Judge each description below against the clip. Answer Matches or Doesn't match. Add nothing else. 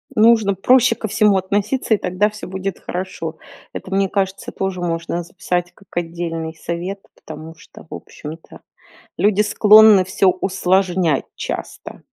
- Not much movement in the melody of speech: Doesn't match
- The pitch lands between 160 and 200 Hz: Matches